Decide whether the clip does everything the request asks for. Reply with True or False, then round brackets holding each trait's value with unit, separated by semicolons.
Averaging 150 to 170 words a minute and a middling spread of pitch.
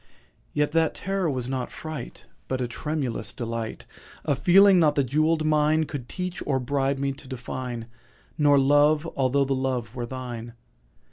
True (155 wpm; 3.3 semitones)